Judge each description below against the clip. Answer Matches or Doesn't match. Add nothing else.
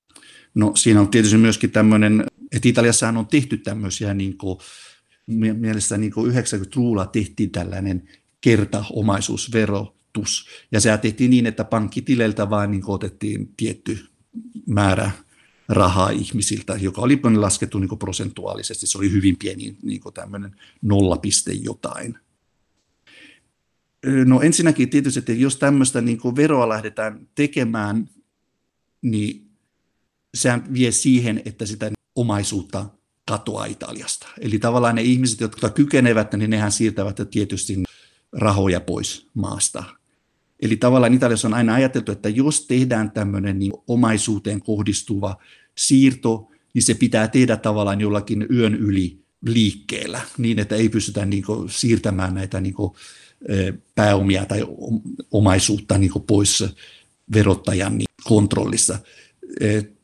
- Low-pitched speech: Matches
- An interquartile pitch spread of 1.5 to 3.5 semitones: Matches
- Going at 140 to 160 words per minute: Doesn't match